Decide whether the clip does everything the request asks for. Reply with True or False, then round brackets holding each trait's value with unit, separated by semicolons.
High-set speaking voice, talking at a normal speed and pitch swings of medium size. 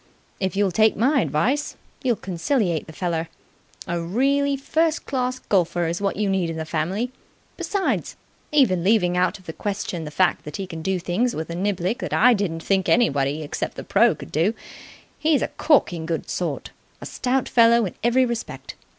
False (195 Hz; 185 wpm; 6.4 semitones)